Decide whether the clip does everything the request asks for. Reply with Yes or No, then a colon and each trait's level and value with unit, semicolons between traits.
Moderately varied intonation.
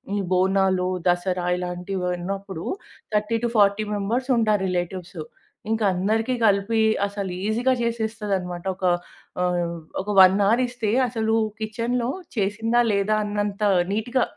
Yes: average, 3.1 semitones